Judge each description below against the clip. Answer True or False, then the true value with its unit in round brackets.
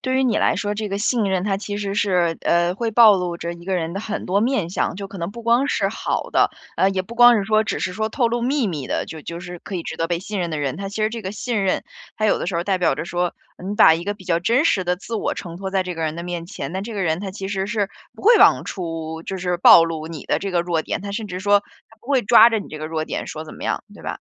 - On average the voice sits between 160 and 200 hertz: True (190 Hz)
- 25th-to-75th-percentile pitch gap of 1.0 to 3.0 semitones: False (3.8 semitones)